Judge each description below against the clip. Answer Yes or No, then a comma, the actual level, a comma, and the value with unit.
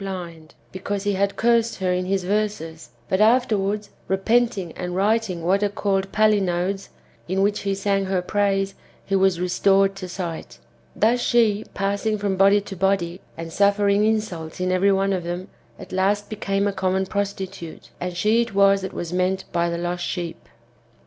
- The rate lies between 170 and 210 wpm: Yes, average, 175 wpm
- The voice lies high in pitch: Yes, high, 195 Hz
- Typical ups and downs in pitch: No, narrow, 2.0 semitones